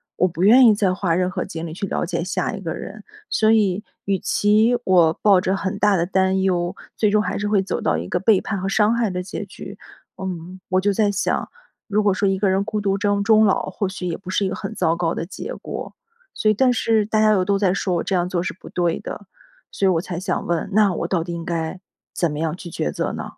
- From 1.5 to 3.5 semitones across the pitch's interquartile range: Yes, average, 2.7 semitones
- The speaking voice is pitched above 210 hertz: No, high, 190 Hz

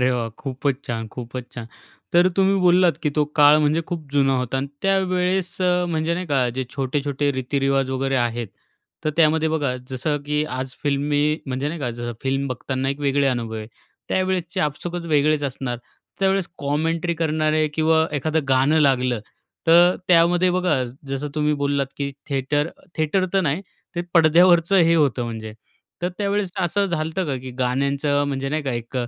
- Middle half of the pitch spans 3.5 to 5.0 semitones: Yes, average, 3.9 semitones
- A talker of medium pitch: Yes, medium, 145 Hz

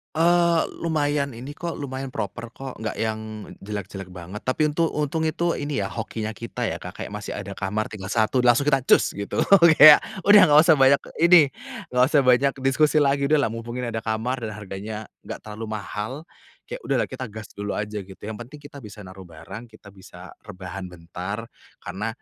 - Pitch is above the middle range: No, low, 115 Hz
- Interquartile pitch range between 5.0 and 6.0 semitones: Yes, wide, 5.6 semitones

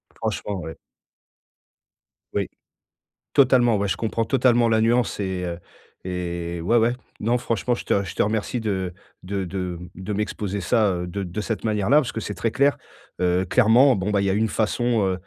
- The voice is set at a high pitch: No, low, 105 Hz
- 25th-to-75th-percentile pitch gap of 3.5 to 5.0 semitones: Yes, average, 3.9 semitones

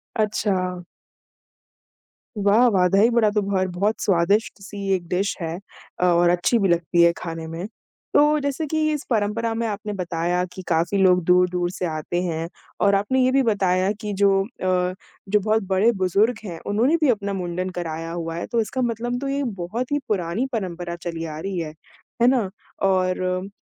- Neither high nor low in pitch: No, high, 195 Hz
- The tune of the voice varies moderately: Yes, average, 3.7 semitones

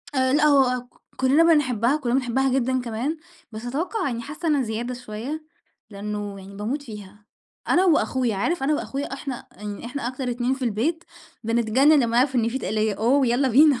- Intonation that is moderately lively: Yes, average, 3.7 semitones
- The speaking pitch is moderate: No, very high, 255 Hz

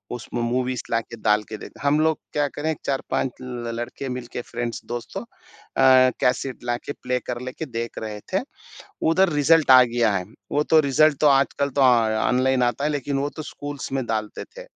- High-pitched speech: No, low, 130 Hz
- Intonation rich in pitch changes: No, average, 3.2 semitones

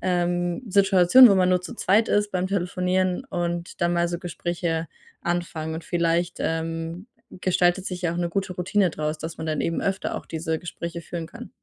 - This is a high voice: No, medium, 175 Hz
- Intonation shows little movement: Yes, narrow, 1.7 semitones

